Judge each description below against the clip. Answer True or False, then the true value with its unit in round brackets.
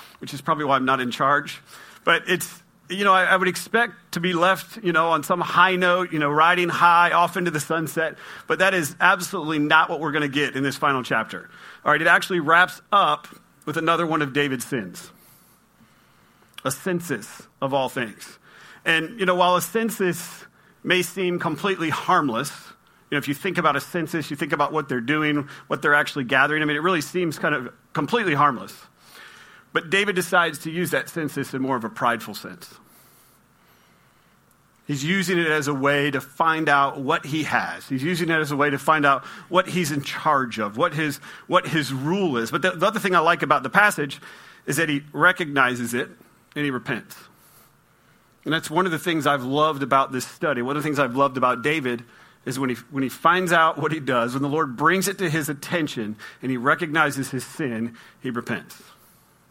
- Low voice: False (155 Hz)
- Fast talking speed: True (210 wpm)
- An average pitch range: True (4.1 semitones)